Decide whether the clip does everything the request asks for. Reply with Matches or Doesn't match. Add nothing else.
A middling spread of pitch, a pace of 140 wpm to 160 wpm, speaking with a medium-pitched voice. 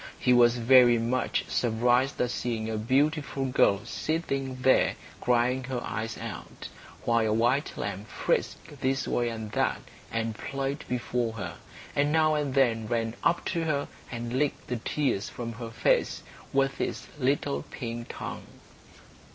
Doesn't match